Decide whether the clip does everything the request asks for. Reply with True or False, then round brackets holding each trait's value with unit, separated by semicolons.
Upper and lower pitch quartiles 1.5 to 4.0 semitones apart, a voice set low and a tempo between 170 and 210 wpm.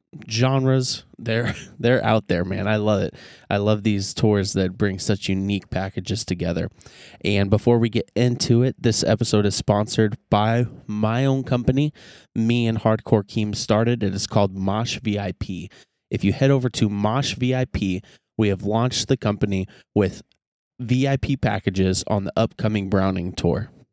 False (3.2 semitones; 110 Hz; 160 wpm)